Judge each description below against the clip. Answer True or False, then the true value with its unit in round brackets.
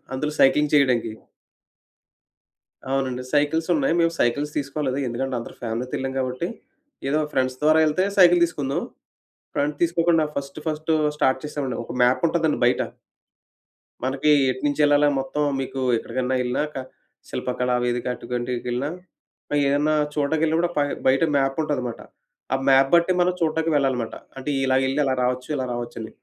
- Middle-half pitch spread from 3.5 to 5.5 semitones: False (3.0 semitones)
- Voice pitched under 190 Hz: True (135 Hz)